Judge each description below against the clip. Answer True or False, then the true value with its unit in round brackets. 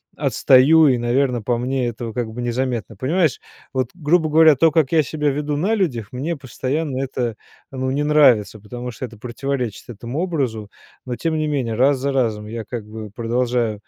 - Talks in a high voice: False (130 Hz)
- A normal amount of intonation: True (3.9 semitones)